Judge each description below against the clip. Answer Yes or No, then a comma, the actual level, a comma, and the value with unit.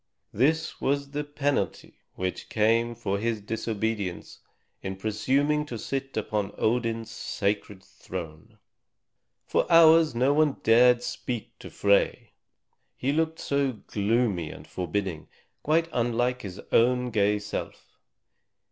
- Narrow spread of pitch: No, average, 4.9 semitones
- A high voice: No, low, 115 Hz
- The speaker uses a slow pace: Yes, slow, 120 wpm